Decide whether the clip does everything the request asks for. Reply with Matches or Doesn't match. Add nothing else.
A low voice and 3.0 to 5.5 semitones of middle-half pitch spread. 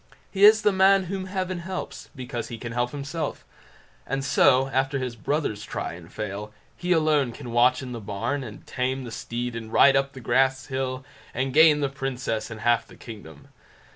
Matches